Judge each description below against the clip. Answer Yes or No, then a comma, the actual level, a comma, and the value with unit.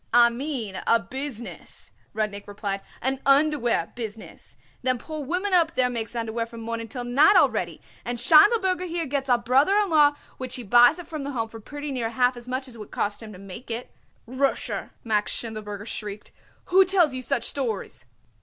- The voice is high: Yes, high, 245 Hz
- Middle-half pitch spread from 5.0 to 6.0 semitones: No, average, 4.4 semitones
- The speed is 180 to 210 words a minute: Yes, average, 190 wpm